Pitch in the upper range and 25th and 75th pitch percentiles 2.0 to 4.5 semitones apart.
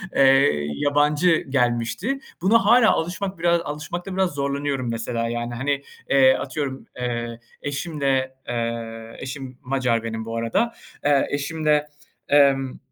No: medium, 140 Hz; average, 4.0 semitones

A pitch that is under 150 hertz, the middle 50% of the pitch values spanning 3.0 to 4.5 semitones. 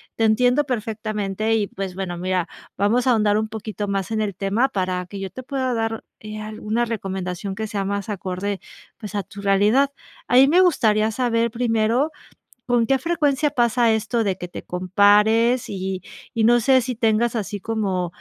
No: high, 215 Hz; average, 3.3 semitones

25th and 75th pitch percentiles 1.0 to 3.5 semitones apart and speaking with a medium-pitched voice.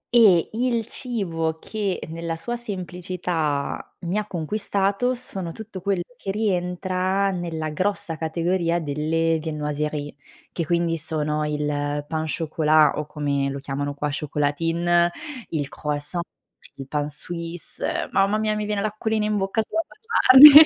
No: average, 4.7 semitones; medium, 170 Hz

